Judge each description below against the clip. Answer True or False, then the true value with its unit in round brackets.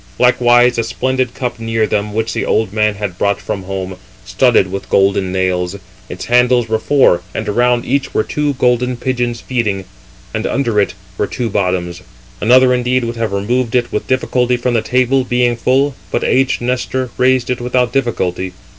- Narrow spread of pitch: False (3.6 semitones)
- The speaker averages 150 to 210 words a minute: True (180 wpm)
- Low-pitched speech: True (120 Hz)